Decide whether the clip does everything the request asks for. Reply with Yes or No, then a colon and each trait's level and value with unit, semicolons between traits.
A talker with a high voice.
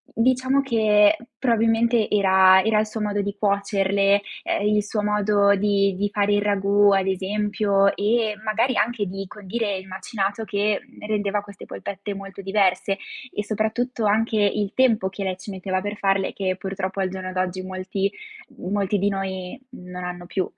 Yes: high, 200 Hz